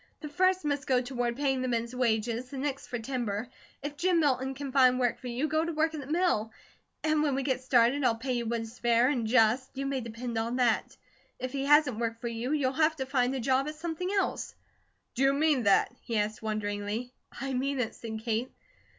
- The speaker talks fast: Yes, fast, 230 wpm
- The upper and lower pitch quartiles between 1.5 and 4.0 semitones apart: Yes, average, 3.5 semitones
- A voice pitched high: Yes, very high, 255 Hz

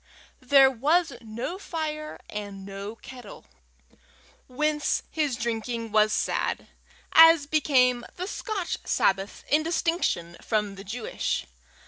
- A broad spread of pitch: Yes, wide, 6.2 semitones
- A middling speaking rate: No, slow, 110 wpm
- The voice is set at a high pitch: Yes, very high, 250 Hz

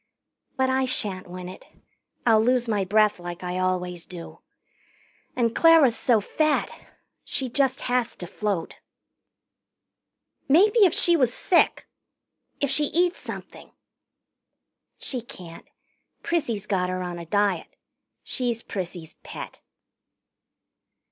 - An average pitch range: No, wide, 6.2 semitones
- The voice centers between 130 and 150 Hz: No, high, 220 Hz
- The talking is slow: Yes, slow, 120 wpm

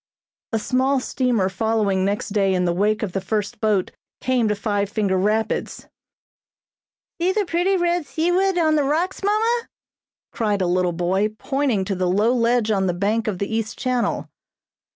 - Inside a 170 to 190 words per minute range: Yes, average, 175 wpm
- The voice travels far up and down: Yes, wide, 5.9 semitones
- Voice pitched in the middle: No, high, 220 Hz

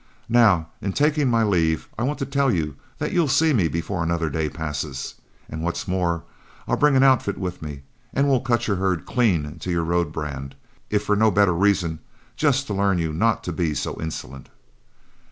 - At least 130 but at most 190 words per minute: No, average, 200 wpm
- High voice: No, very low, 90 Hz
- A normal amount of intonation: No, wide, 6.5 semitones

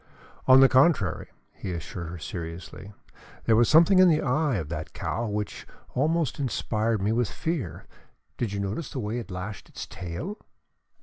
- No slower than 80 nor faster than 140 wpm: No, average, 170 wpm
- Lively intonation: Yes, wide, 7.1 semitones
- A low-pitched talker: Yes, low, 110 Hz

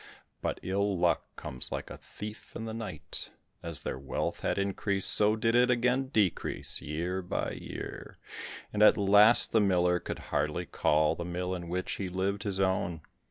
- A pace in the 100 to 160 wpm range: No, average, 175 wpm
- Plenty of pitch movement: No, average, 3.3 semitones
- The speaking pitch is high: No, very low, 95 Hz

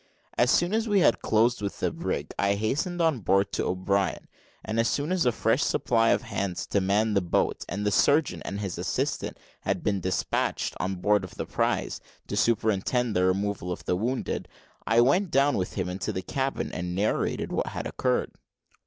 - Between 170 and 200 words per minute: Yes, average, 195 wpm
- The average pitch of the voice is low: Yes, low, 105 Hz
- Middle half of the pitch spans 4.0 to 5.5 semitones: Yes, average, 4.7 semitones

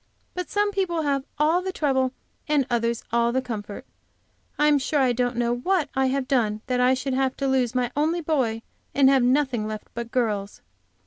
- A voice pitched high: Yes, very high, 260 Hz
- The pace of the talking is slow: No, average, 200 wpm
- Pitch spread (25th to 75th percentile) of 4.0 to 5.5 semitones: No, average, 3.6 semitones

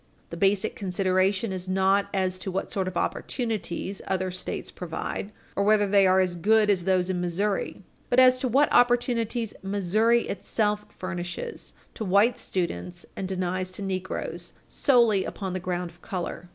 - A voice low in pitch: No, high, 190 Hz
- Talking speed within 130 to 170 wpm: Yes, average, 165 wpm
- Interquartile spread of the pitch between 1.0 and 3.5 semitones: Yes, narrow, 2.4 semitones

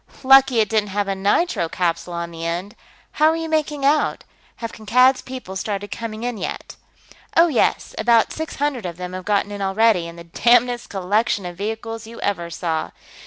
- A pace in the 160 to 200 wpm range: Yes, average, 190 wpm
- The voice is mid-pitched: No, high, 215 Hz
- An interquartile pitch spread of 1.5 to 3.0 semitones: No, average, 4.9 semitones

